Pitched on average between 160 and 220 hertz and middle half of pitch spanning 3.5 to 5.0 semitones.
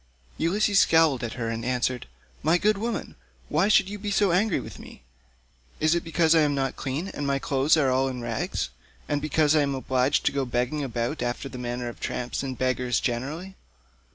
No: medium, 140 Hz; average, 4.7 semitones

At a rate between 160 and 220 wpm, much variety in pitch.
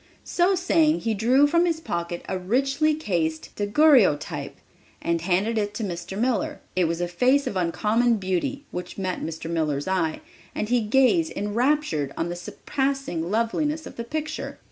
Yes: average, 165 wpm; wide, 8.0 semitones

